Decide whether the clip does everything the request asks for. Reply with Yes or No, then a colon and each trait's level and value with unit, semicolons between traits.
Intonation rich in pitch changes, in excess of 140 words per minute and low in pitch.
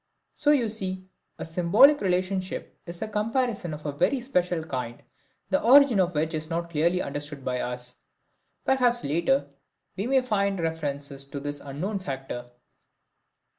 No: wide, 6.7 semitones; average, 155 wpm; medium, 175 Hz